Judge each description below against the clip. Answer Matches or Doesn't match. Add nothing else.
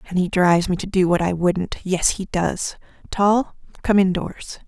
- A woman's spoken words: Matches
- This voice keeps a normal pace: Matches